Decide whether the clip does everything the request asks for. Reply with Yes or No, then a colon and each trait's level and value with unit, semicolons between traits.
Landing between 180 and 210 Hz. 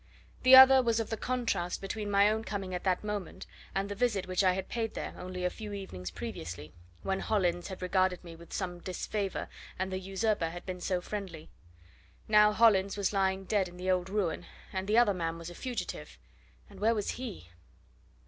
Yes: high, 190 Hz